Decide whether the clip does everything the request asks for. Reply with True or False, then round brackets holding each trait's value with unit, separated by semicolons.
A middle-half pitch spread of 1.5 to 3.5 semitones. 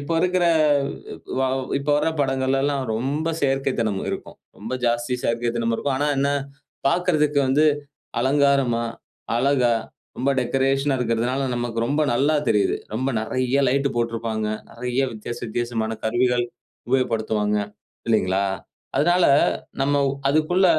True (3.2 semitones)